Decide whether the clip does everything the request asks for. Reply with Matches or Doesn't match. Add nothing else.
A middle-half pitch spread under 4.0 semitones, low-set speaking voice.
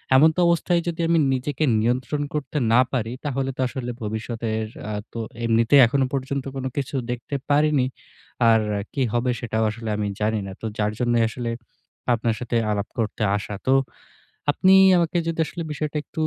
Doesn't match